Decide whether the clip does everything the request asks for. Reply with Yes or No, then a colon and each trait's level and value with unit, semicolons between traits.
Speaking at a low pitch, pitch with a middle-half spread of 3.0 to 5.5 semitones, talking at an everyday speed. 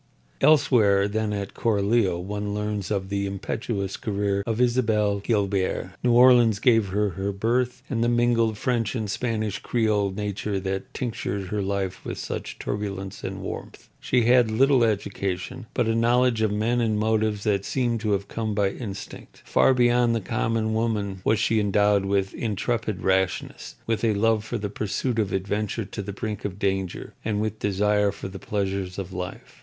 No: low, 105 Hz; narrow, 2.5 semitones; average, 170 wpm